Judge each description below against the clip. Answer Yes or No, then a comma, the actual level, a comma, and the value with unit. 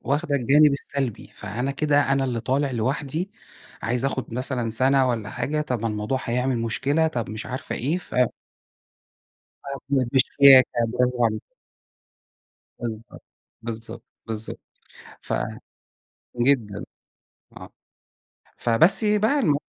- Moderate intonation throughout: Yes, average, 3.5 semitones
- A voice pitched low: Yes, low, 130 Hz